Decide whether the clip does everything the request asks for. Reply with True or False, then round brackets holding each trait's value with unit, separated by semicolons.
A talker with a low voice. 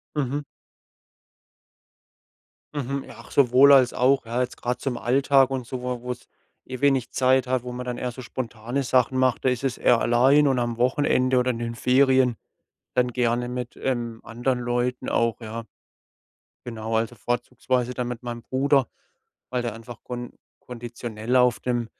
True (125 Hz)